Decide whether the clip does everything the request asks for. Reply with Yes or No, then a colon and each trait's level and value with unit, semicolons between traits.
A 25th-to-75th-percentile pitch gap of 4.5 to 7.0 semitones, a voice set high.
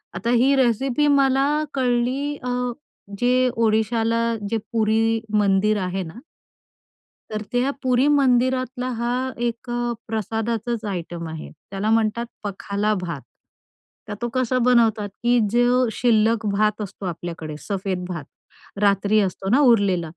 No: average, 3.5 semitones; high, 225 Hz